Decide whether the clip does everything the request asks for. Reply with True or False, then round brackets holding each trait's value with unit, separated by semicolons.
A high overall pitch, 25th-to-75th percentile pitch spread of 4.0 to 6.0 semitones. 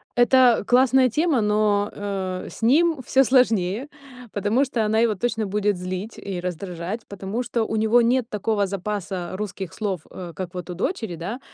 True (210 Hz; 4.3 semitones)